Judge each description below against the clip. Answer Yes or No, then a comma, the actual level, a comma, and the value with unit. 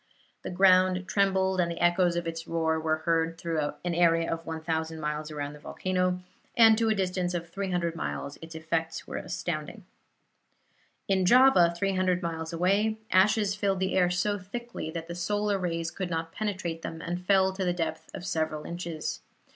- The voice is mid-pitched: Yes, medium, 175 Hz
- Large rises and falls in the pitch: No, narrow, 2.6 semitones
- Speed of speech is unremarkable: Yes, average, 180 wpm